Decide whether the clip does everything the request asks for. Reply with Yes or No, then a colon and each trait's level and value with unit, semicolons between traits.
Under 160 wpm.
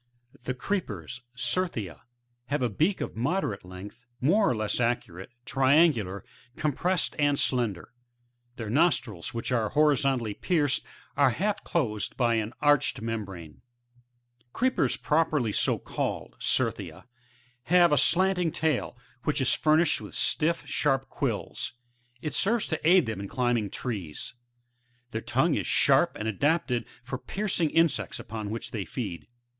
Yes: average, 150 wpm